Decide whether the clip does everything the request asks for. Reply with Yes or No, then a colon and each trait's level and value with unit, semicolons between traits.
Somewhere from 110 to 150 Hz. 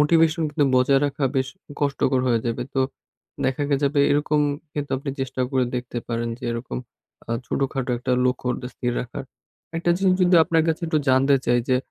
Yes: low, 135 Hz